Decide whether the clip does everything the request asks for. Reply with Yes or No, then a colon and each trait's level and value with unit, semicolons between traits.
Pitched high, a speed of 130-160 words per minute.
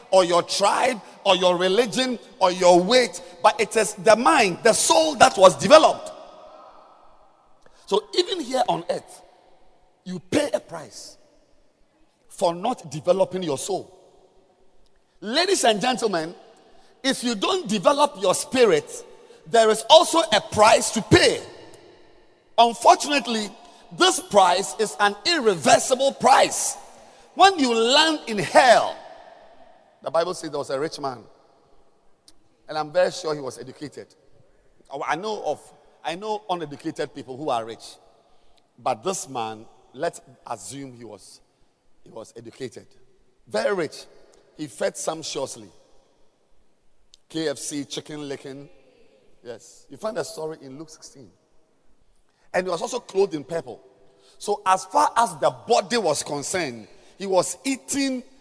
Yes: high, 205 Hz; slow, 135 wpm